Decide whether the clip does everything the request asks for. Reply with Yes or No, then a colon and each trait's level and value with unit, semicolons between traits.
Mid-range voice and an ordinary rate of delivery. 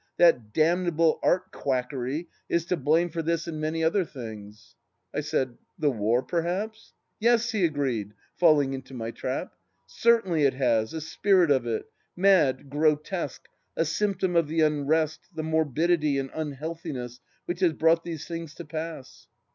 Yes: medium, 155 Hz; average, 170 wpm